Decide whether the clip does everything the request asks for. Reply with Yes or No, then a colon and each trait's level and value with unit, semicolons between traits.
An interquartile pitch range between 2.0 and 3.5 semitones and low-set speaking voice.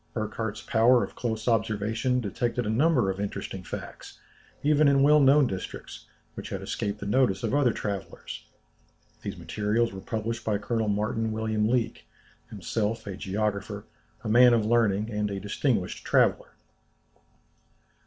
Yes: average, 2.7 semitones; low, 110 Hz